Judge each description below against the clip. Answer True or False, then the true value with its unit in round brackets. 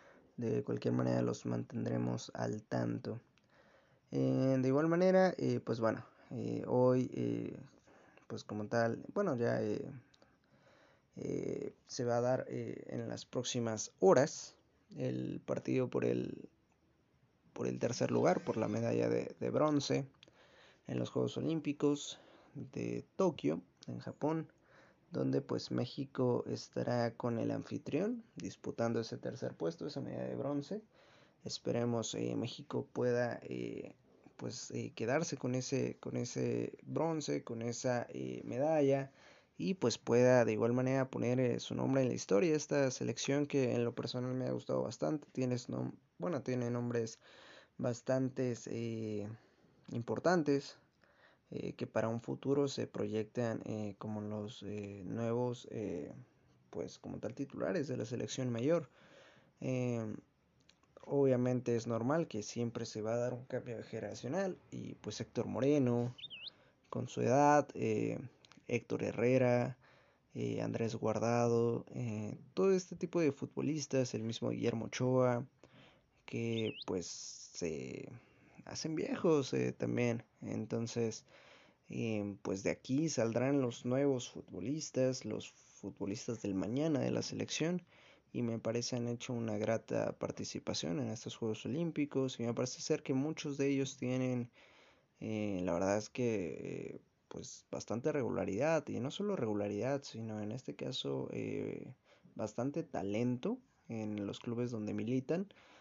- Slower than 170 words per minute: True (140 wpm)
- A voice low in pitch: True (120 Hz)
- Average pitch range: True (4.3 semitones)